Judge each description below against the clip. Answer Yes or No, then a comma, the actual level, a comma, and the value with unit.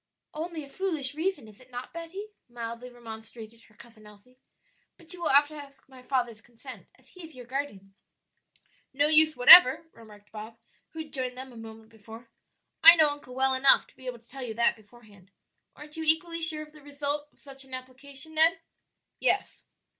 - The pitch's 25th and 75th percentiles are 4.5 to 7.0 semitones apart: Yes, average, 4.8 semitones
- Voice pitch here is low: No, very high, 265 Hz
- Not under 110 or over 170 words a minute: No, average, 195 wpm